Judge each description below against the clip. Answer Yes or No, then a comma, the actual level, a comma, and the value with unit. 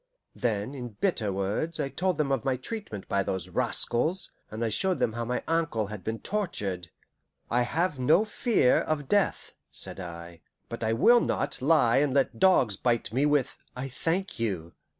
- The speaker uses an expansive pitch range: Yes, wide, 7.1 semitones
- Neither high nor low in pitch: No, low, 125 Hz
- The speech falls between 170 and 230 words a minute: Yes, average, 180 wpm